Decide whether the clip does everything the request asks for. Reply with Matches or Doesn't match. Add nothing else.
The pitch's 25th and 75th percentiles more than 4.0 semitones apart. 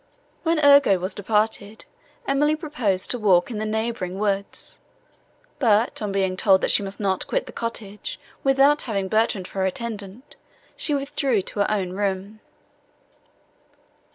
Matches